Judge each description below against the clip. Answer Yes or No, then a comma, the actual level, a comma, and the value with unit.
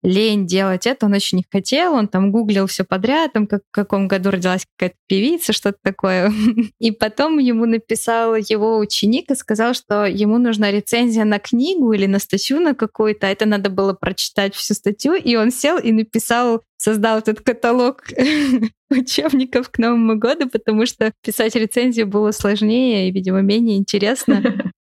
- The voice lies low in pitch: No, high, 220 Hz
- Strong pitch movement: No, average, 3.1 semitones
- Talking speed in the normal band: No, fast, 165 wpm